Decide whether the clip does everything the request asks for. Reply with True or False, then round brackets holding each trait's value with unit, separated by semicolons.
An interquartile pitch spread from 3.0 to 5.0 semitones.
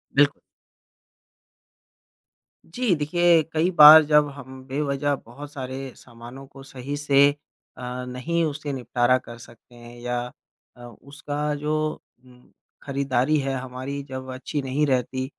False (2.5 semitones)